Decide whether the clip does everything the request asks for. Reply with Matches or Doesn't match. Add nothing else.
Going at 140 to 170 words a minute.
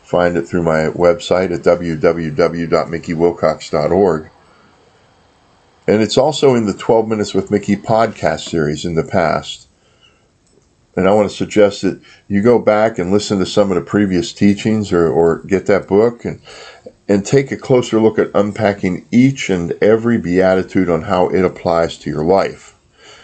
Matches